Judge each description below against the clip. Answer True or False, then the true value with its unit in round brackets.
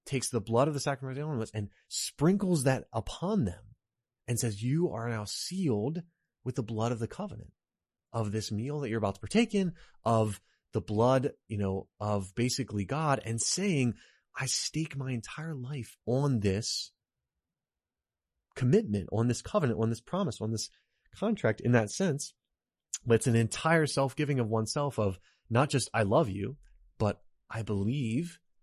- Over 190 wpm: False (170 wpm)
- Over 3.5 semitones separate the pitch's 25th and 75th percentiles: True (4.4 semitones)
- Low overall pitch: True (120 Hz)